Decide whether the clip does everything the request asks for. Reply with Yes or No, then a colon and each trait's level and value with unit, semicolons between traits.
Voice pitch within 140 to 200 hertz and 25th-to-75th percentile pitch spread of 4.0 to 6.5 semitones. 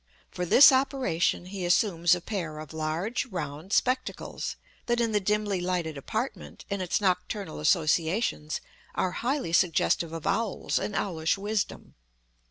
Yes: medium, 185 Hz; average, 4.6 semitones